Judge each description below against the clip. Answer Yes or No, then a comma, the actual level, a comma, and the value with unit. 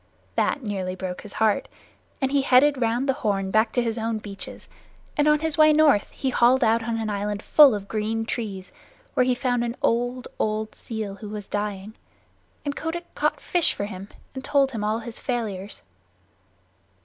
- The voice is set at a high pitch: Yes, high, 225 Hz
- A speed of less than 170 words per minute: No, average, 185 wpm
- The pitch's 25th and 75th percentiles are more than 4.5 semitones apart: No, average, 4.0 semitones